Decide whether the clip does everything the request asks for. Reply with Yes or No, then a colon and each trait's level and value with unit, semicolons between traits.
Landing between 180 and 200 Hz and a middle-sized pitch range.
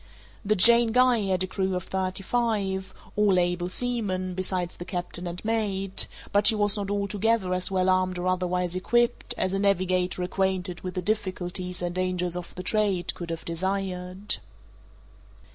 No: medium, 185 Hz; narrow, 2.0 semitones